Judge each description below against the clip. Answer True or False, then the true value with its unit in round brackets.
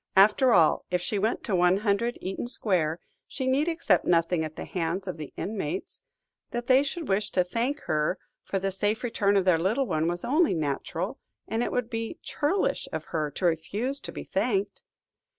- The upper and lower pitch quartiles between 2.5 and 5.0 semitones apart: False (5.4 semitones)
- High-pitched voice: True (200 Hz)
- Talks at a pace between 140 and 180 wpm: False (190 wpm)